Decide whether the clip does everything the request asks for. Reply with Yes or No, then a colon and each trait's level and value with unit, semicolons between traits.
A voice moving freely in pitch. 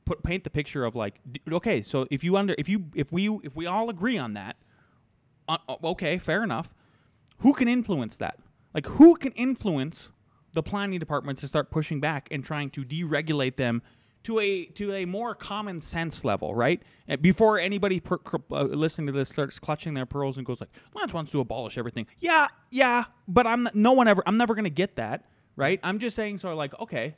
Yes: wide, 6.7 semitones